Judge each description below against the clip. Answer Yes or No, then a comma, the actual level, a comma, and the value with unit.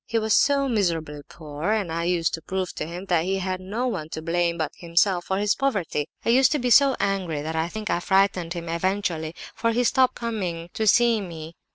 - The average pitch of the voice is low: No, medium, 185 Hz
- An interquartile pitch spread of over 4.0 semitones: Yes, average, 4.6 semitones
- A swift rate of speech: Yes, fast, 225 wpm